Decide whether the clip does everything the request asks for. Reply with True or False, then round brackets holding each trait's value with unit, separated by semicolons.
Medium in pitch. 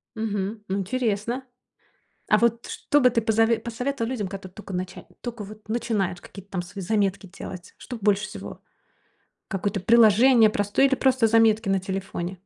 False (215 Hz)